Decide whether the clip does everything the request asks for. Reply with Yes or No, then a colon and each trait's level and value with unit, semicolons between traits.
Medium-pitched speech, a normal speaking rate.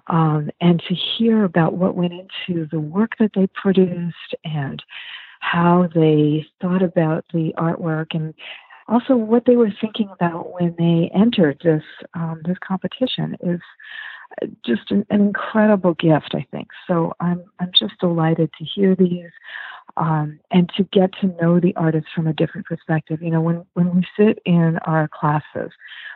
Yes: medium, 175 Hz; average, 165 wpm